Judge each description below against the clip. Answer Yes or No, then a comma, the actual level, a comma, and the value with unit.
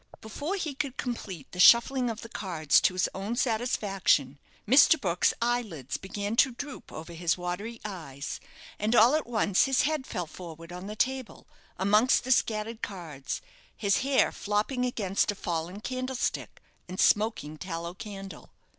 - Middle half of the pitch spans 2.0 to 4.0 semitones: No, wide, 5.5 semitones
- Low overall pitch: No, high, 210 Hz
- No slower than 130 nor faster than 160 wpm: Yes, average, 155 wpm